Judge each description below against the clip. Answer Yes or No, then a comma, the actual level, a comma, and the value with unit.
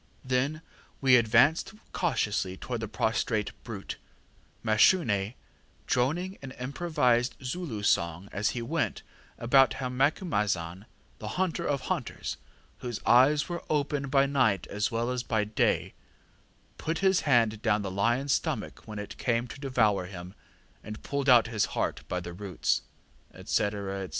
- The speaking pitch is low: Yes, low, 120 Hz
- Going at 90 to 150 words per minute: Yes, average, 145 wpm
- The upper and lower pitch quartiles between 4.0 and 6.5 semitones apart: Yes, average, 4.9 semitones